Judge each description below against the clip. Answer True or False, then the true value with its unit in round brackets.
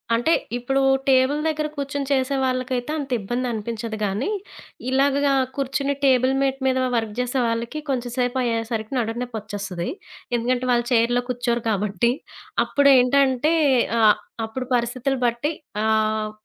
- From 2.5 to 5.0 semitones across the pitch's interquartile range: True (2.9 semitones)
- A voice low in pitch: False (245 Hz)